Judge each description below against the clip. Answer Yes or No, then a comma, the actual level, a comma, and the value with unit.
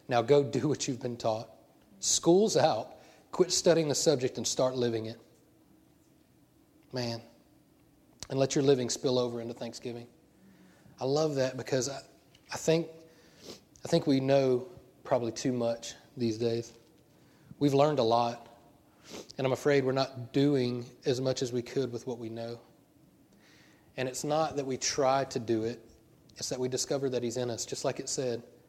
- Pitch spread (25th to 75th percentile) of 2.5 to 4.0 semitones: Yes, average, 3.4 semitones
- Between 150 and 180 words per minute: Yes, average, 170 wpm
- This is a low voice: Yes, low, 130 Hz